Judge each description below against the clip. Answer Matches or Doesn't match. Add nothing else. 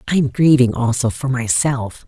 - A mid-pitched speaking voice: Doesn't match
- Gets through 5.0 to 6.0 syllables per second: Doesn't match